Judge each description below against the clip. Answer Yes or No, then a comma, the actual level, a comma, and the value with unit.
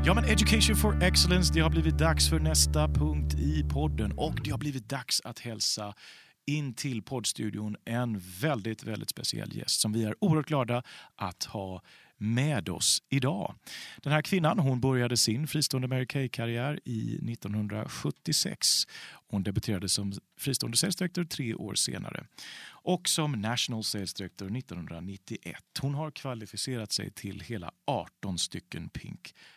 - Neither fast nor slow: Yes, average, 145 wpm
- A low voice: Yes, low, 110 Hz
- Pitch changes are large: Yes, wide, 6.2 semitones